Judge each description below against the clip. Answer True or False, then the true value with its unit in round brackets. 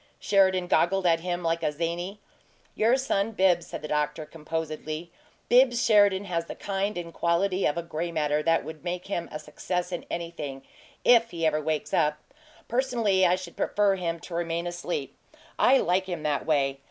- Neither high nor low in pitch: True (175 Hz)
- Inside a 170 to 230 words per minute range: True (180 wpm)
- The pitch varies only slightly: False (3.2 semitones)